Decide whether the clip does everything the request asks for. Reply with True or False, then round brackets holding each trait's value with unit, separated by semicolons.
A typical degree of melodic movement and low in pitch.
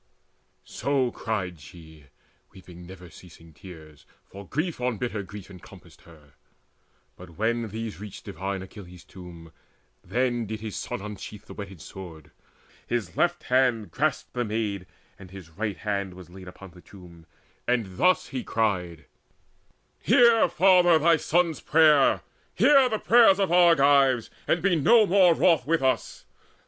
False (8.3 semitones; 105 Hz)